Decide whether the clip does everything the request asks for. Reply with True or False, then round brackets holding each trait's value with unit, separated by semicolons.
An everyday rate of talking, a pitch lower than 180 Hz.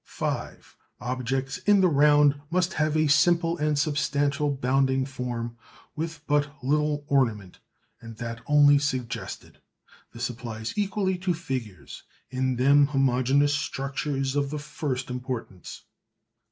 False (125 wpm; 140 Hz)